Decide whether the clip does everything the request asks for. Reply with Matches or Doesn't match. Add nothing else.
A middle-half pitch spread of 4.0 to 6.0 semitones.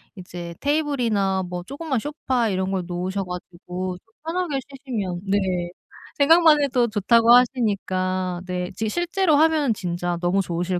Doesn't match